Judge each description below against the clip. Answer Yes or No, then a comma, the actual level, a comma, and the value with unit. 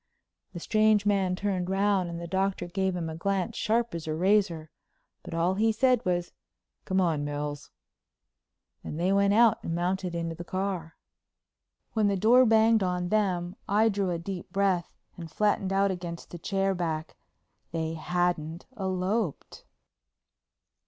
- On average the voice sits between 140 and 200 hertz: Yes, medium, 185 Hz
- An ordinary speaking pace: Yes, average, 155 wpm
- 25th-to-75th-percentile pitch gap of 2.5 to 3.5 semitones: Yes, average, 2.8 semitones